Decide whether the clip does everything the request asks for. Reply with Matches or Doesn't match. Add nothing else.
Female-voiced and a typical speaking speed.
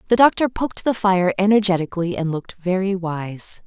Matches